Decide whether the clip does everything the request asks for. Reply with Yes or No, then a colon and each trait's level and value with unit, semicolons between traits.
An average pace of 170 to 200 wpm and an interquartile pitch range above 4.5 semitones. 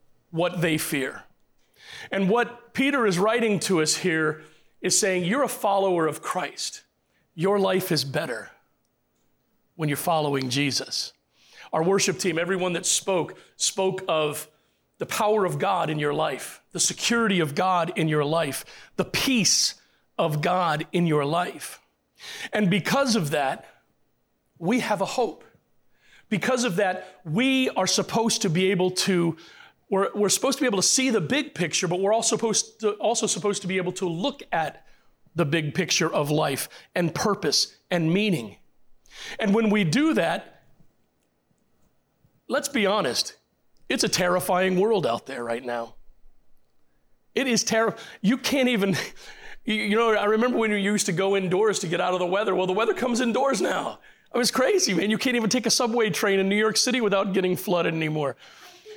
Yes: average, 175 wpm; average, 5.0 semitones